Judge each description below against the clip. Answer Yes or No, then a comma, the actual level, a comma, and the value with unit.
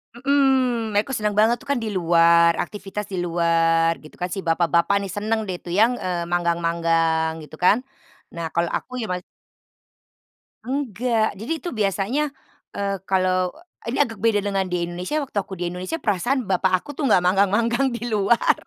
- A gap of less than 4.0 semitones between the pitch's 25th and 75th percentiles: No, average, 4.8 semitones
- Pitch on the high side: Yes, high, 195 Hz